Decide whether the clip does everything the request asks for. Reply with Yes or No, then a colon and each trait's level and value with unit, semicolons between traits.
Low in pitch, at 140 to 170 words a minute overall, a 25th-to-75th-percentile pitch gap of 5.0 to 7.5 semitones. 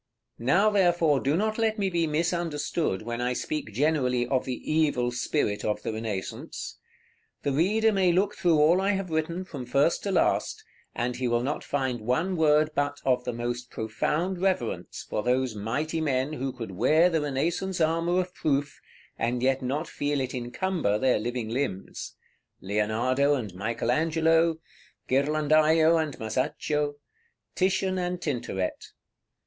No: medium, 145 Hz; average, 160 wpm; wide, 5.4 semitones